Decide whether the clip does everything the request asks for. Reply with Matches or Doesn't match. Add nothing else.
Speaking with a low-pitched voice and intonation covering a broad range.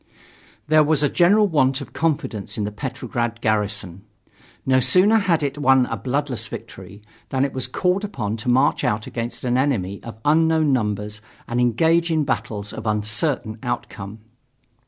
Matches